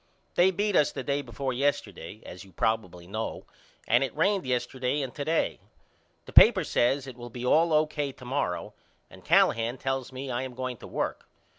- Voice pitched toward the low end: Yes, low, 130 Hz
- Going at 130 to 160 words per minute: No, average, 190 wpm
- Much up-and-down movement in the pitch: No, average, 3.2 semitones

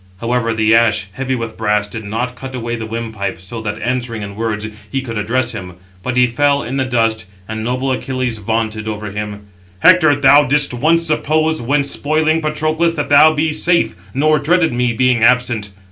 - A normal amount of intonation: Yes, average, 4.5 semitones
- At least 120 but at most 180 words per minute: No, average, 190 wpm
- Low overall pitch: Yes, low, 125 Hz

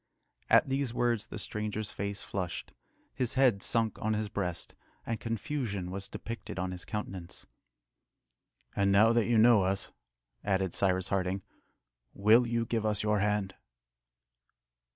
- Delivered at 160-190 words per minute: No, average, 140 wpm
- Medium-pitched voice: No, low, 105 Hz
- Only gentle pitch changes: No, average, 3.0 semitones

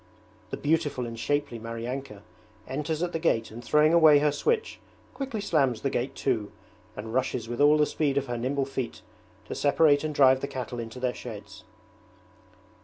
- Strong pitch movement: No, average, 4.0 semitones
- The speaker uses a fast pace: No, average, 180 wpm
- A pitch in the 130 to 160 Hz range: Yes, low, 135 Hz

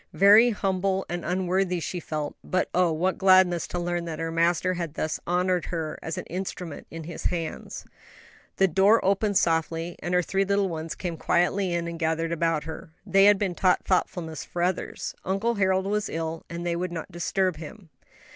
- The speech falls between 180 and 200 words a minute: Yes, average, 190 wpm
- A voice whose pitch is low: No, medium, 175 Hz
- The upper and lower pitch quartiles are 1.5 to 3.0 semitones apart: Yes, narrow, 2.5 semitones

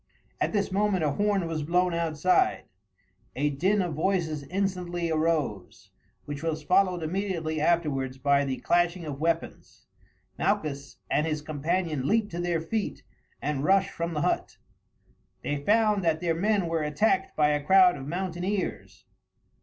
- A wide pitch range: No, average, 3.9 semitones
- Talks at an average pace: Yes, average, 150 wpm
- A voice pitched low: No, medium, 165 Hz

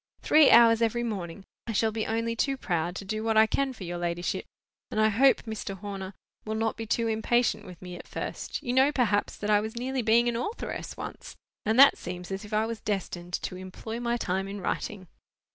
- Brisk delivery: Yes, fast, 220 wpm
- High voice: Yes, high, 220 Hz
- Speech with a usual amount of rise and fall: Yes, average, 3.4 semitones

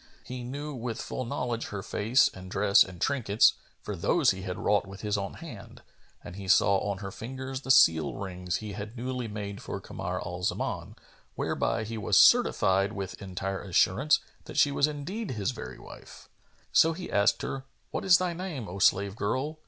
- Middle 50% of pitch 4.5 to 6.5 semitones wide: Yes, average, 5.2 semitones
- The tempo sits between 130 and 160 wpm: No, average, 190 wpm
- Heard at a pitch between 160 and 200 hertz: No, low, 105 Hz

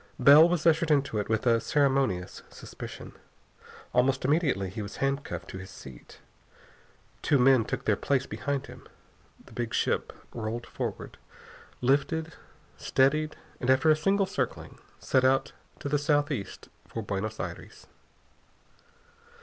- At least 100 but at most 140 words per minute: Yes, slow, 135 wpm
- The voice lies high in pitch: No, low, 135 Hz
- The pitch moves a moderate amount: Yes, average, 4.8 semitones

